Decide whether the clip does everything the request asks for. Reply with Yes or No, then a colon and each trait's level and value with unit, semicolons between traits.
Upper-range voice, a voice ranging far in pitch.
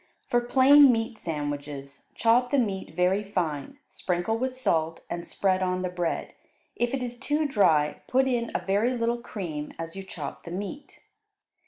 Yes: high, 200 Hz; wide, 6.4 semitones